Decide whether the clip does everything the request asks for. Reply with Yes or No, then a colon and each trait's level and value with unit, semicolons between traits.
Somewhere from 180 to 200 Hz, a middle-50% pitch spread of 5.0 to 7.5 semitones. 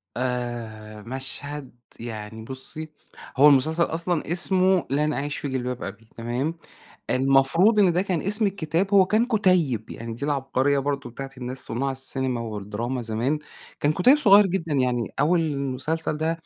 No: medium, 140 Hz; average, 5.3 semitones